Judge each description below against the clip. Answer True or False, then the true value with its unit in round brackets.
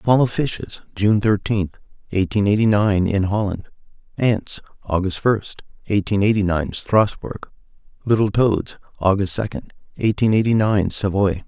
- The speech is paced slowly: True (130 wpm)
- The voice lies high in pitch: False (100 Hz)